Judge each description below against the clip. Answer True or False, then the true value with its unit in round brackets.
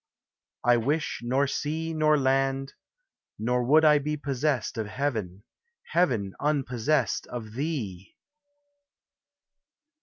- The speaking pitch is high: False (135 Hz)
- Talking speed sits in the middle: False (100 wpm)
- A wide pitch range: False (4.1 semitones)